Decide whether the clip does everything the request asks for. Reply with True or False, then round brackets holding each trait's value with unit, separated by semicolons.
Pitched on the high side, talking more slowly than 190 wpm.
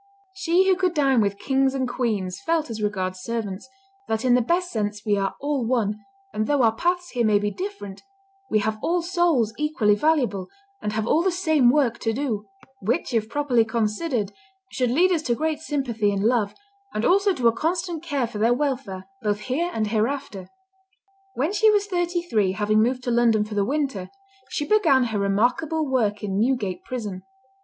False (245 Hz; 195 wpm)